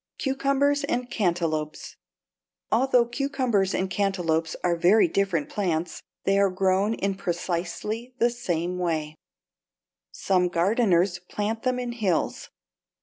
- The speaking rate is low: Yes, slow, 115 wpm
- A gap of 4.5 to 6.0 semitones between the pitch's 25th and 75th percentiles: Yes, wide, 5.5 semitones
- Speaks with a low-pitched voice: No, high, 195 Hz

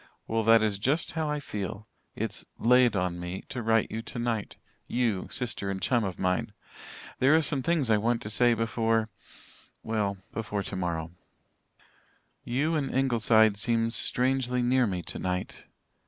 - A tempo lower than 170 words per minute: Yes, average, 155 wpm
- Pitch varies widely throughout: No, average, 3.6 semitones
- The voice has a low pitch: Yes, low, 115 Hz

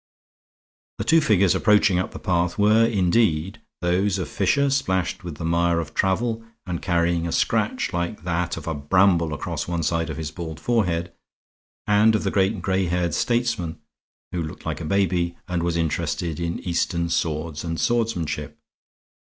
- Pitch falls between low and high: No, very low, 90 Hz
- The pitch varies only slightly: No, average, 3.1 semitones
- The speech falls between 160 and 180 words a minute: Yes, average, 170 wpm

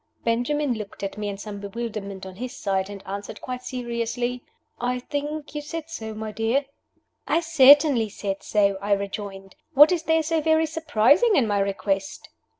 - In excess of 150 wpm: Yes, average, 170 wpm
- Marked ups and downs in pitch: Yes, wide, 6.5 semitones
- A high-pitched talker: Yes, high, 235 Hz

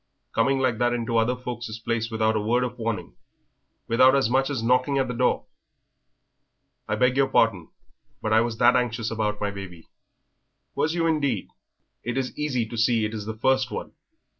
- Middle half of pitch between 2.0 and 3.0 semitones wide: Yes, narrow, 2.5 semitones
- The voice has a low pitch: Yes, low, 120 Hz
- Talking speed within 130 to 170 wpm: No, average, 190 wpm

